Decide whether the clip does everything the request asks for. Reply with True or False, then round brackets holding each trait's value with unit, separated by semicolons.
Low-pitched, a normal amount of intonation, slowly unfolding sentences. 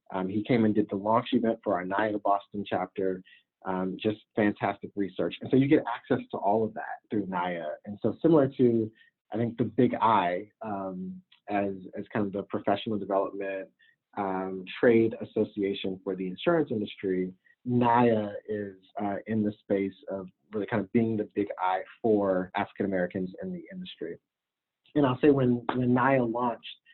False (105 Hz; 3.5 semitones; 175 wpm)